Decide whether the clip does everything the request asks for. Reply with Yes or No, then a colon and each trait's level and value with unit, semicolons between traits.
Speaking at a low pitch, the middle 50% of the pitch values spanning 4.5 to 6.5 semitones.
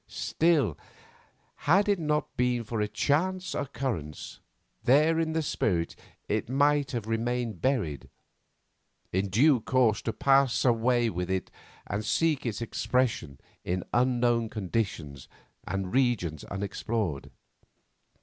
Yes: low, 120 Hz; wide, 5.5 semitones